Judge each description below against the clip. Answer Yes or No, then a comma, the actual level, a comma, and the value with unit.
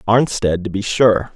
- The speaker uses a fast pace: No, average, 175 wpm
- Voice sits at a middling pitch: No, low, 105 Hz